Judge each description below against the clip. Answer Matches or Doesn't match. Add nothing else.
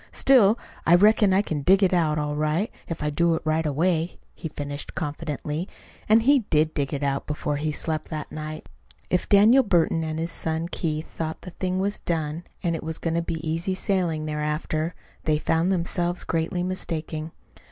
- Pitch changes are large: Doesn't match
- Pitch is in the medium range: Matches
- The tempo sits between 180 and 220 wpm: Matches